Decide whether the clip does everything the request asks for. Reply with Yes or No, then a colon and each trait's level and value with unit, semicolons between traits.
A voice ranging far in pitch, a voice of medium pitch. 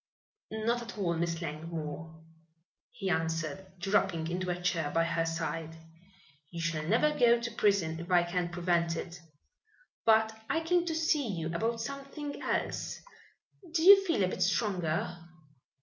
Yes: wide, 5.7 semitones; medium, 180 Hz